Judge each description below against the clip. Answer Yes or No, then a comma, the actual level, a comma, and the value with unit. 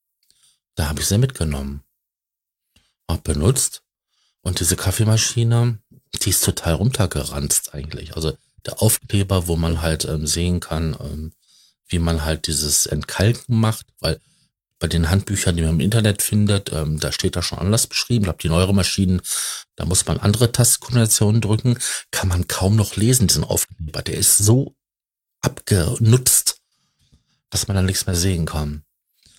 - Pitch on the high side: No, very low, 95 Hz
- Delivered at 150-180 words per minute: Yes, average, 155 wpm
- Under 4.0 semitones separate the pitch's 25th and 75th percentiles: No, average, 5.1 semitones